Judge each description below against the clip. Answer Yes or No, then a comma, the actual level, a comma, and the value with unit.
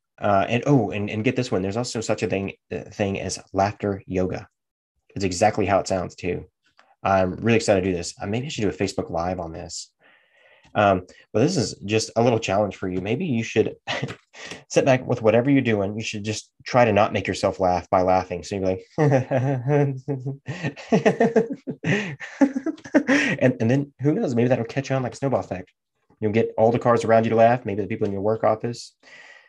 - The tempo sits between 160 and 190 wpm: No, fast, 205 wpm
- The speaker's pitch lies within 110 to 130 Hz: Yes, low, 115 Hz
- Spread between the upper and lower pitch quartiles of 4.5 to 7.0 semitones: Yes, average, 4.8 semitones